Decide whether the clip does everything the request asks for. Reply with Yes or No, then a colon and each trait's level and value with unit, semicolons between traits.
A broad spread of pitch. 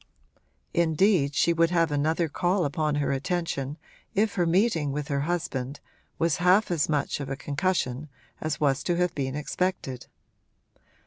No: average, 3.8 semitones